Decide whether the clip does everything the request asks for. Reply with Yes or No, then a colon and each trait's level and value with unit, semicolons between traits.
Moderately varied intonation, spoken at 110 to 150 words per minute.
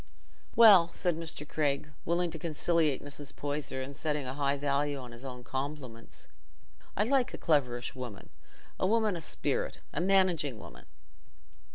Yes: average, 4.0 semitones; average, 145 wpm